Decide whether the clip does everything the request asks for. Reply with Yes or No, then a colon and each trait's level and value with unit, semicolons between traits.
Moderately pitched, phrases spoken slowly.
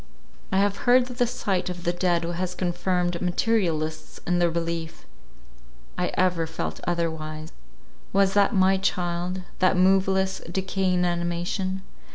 Yes: medium, 180 Hz; slow, 130 wpm